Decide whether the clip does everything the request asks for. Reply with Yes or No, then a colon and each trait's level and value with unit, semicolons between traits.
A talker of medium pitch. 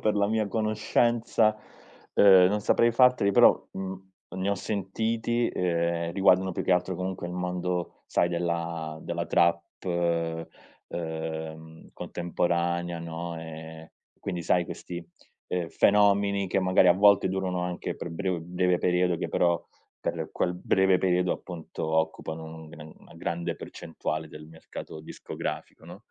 No: very low, 90 Hz